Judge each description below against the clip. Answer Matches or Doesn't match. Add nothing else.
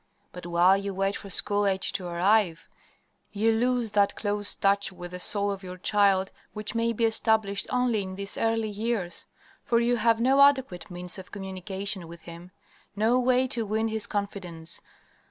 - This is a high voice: Matches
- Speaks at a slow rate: Doesn't match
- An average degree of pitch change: Matches